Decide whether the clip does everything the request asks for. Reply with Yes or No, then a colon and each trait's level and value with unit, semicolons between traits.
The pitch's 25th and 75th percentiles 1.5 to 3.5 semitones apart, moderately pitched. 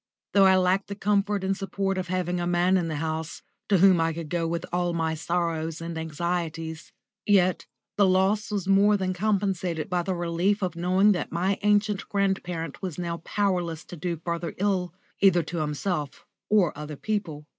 Yes: average, 2.8 semitones; medium, 180 Hz